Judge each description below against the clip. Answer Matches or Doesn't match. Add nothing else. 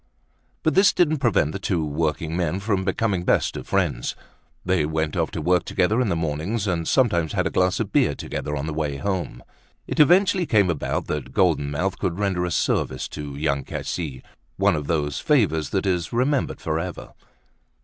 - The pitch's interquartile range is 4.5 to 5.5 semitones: Matches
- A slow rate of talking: Doesn't match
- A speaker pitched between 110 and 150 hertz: Doesn't match